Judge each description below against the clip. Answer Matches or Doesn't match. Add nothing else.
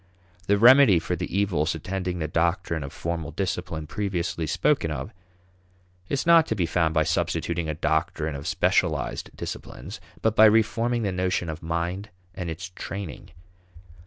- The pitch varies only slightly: Doesn't match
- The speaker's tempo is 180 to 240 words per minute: Doesn't match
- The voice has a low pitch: Matches